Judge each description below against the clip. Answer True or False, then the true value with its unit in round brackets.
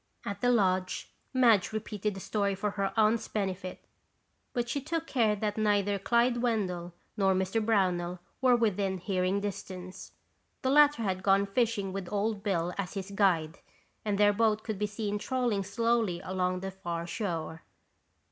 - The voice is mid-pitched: False (200 Hz)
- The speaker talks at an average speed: True (160 wpm)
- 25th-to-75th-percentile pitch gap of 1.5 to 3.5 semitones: True (2.9 semitones)